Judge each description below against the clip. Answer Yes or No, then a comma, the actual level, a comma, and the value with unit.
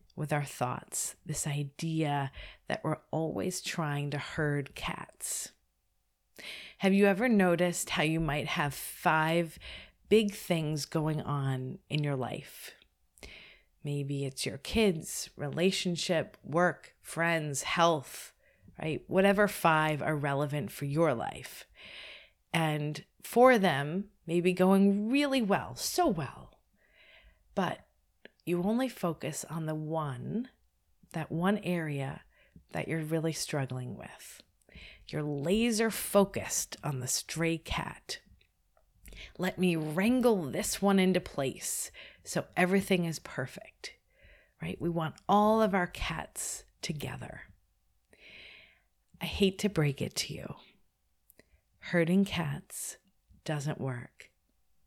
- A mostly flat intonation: No, average, 4.5 semitones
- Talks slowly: Yes, slow, 115 wpm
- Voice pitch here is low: No, medium, 165 Hz